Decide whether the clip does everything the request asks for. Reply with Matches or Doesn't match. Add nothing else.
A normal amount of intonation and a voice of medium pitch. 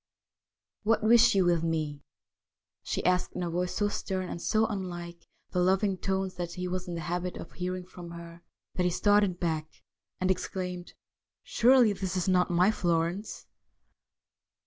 Doesn't match